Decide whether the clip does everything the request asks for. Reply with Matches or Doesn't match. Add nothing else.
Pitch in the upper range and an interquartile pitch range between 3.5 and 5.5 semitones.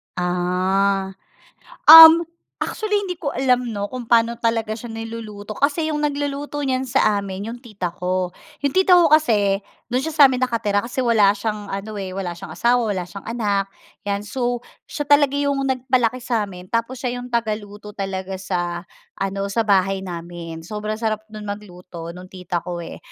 Matches